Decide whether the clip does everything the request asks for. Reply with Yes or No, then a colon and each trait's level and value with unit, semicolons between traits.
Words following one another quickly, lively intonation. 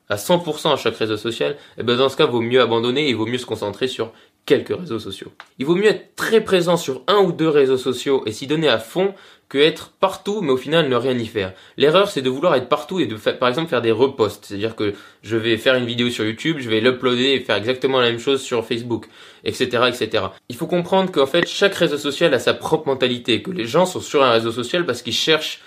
Yes: fast, 260 wpm; wide, 5.9 semitones